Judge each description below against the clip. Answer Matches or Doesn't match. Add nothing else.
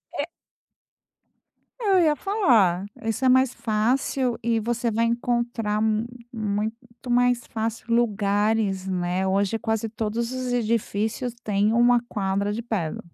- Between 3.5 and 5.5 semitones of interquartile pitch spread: Doesn't match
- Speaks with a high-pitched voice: Matches